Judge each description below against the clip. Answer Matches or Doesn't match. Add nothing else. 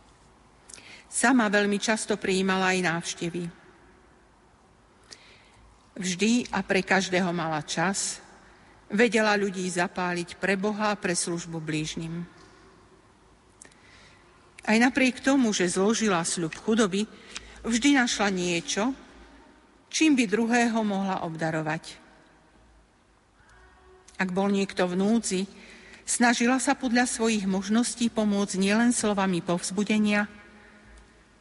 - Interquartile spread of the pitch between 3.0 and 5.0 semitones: Matches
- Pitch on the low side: Doesn't match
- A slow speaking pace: Matches